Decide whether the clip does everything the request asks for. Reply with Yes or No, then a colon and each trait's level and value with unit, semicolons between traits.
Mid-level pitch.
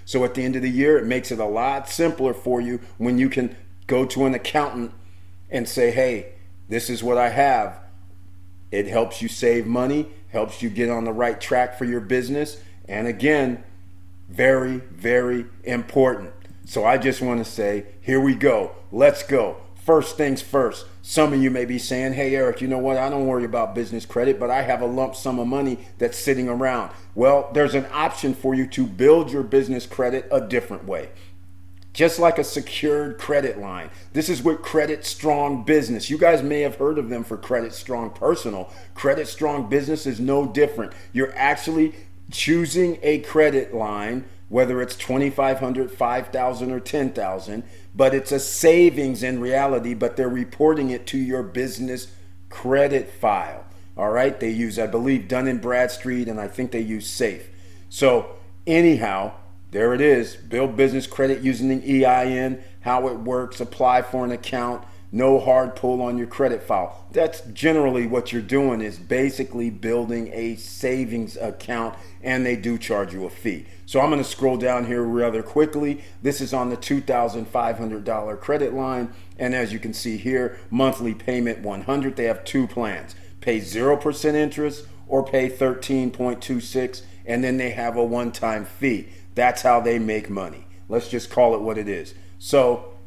No: low, 125 Hz